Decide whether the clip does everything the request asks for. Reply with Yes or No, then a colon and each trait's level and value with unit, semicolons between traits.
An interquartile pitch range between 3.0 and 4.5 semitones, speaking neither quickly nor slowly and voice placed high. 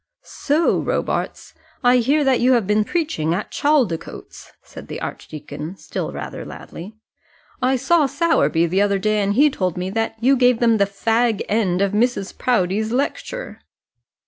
No: average, 5.1 semitones; average, 160 wpm; high, 225 Hz